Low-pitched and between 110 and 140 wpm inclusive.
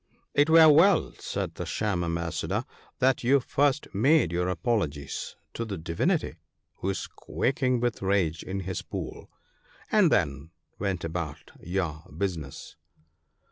Yes: very low, 95 Hz; slow, 135 wpm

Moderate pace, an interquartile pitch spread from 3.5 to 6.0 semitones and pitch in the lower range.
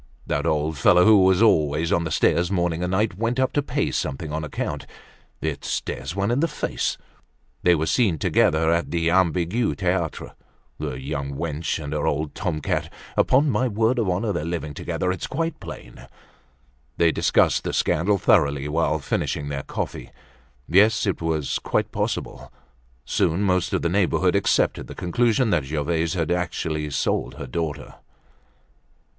Yes: average, 165 wpm; average, 4.3 semitones; very low, 85 Hz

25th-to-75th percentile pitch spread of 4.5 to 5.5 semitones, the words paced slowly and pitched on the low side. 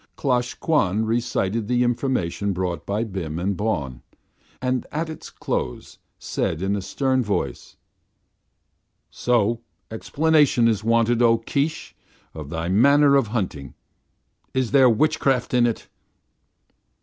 Yes: average, 4.9 semitones; slow, 125 wpm; low, 115 Hz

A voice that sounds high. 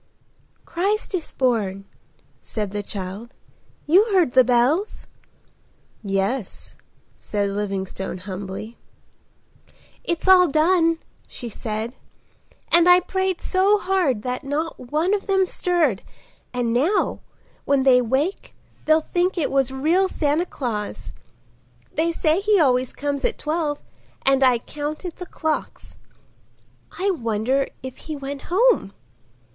Yes: very high, 285 Hz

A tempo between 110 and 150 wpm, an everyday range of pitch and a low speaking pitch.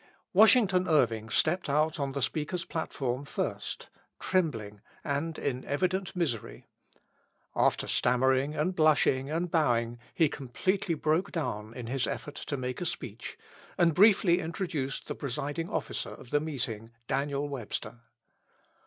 No: slow, 135 wpm; average, 4.8 semitones; medium, 145 Hz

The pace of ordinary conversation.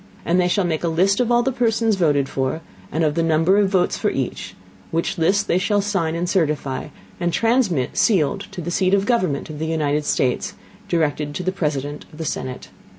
No: fast, 215 wpm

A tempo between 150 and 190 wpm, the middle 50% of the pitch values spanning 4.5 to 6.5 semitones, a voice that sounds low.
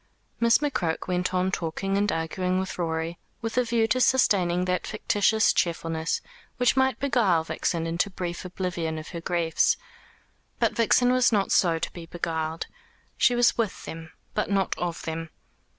No: average, 165 wpm; average, 5.2 semitones; medium, 180 Hz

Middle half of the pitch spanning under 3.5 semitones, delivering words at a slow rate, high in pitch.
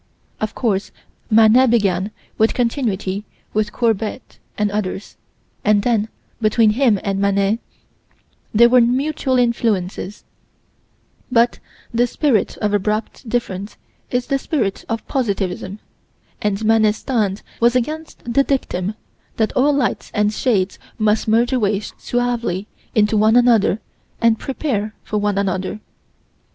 Yes: average, 3.0 semitones; slow, 125 wpm; high, 220 Hz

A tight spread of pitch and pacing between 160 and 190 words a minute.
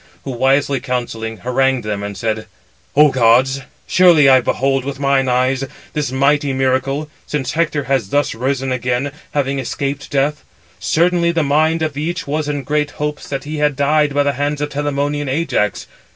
Yes: narrow, 2.1 semitones; average, 170 wpm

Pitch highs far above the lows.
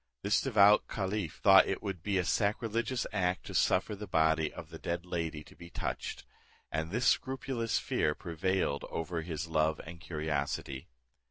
No: average, 4.5 semitones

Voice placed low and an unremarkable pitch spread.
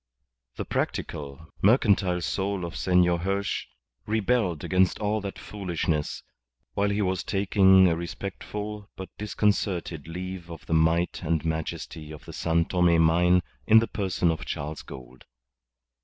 Yes: very low, 90 Hz; average, 3.3 semitones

